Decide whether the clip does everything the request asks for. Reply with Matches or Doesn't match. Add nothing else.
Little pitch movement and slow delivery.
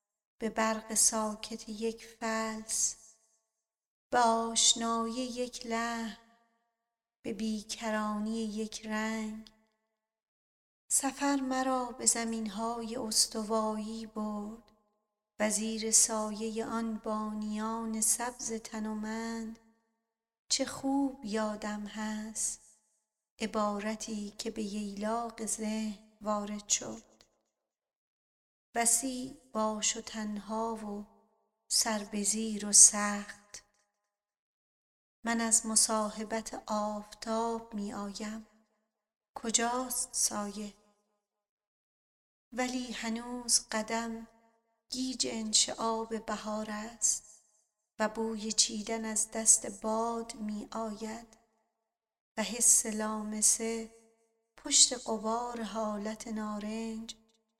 Matches